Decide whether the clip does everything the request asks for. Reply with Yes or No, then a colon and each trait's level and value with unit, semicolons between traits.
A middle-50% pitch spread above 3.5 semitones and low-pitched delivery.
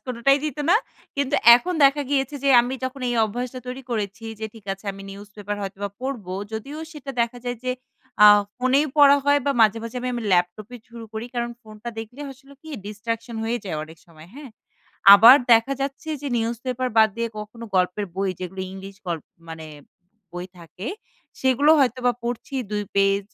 No: average, 4.4 semitones; high, 230 Hz